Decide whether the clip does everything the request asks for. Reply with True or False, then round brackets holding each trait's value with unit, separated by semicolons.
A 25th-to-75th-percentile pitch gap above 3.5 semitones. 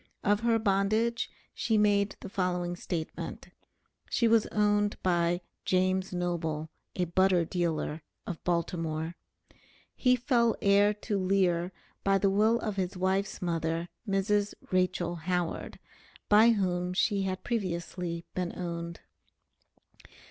False (2.9 semitones)